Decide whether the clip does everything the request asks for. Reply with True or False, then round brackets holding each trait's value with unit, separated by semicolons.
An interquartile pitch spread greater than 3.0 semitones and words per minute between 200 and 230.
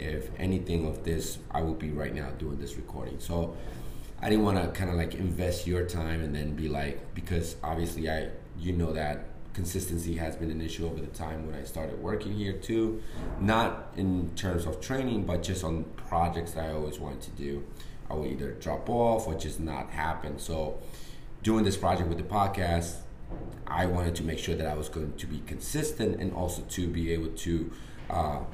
False (2.7 semitones; 205 wpm)